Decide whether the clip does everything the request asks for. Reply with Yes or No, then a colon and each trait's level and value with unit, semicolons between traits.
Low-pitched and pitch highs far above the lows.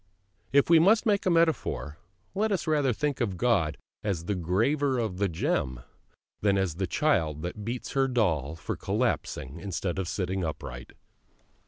Yes: low, 100 Hz; wide, 8.8 semitones